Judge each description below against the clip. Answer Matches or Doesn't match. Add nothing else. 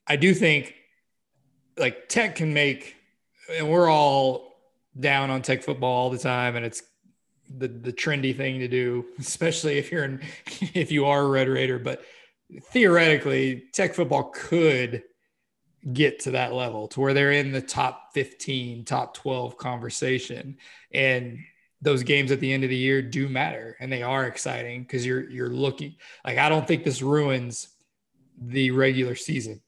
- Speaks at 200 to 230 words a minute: Doesn't match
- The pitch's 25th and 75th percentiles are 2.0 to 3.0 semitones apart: Matches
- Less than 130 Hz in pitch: Doesn't match